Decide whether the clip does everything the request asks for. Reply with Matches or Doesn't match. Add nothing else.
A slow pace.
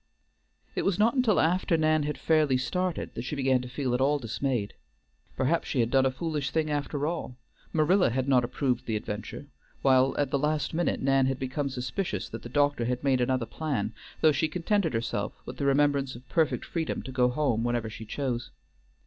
Doesn't match